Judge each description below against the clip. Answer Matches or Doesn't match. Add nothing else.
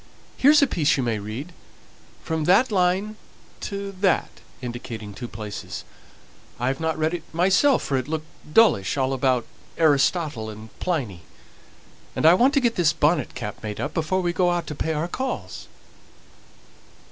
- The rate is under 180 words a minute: Matches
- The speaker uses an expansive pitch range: Matches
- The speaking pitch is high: Doesn't match